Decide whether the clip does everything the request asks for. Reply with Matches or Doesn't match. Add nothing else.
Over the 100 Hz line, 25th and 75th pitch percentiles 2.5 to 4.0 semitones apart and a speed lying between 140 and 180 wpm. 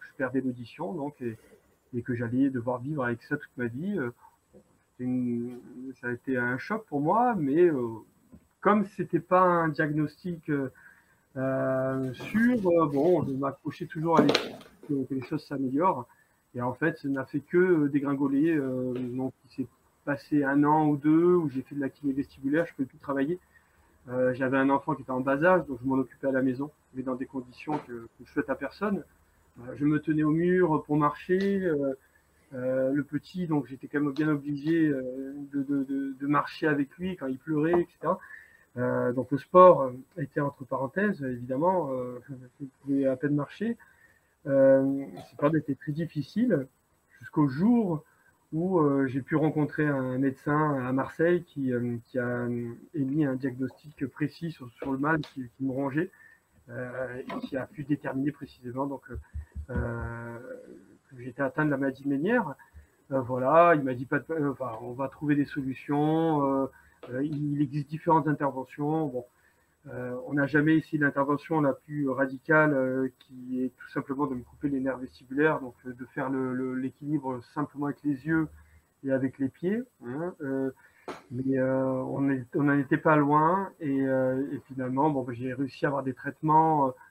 Matches